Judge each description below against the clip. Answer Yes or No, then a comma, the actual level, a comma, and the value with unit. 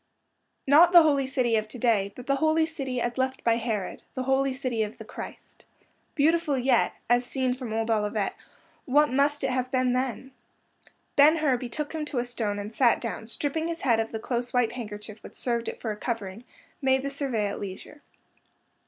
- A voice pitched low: No, very high, 250 Hz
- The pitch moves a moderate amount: Yes, average, 3.5 semitones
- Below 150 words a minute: No, average, 195 wpm